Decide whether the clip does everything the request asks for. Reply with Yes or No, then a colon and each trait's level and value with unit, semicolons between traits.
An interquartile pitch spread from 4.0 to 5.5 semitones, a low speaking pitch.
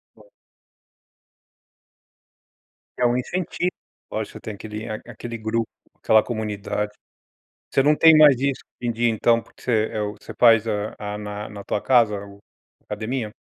No: average, 2.8 semitones; low, 115 Hz